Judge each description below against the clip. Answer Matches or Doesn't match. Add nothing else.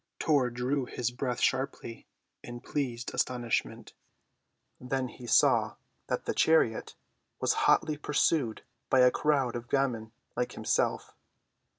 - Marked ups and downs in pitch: Doesn't match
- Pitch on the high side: Doesn't match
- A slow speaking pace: Matches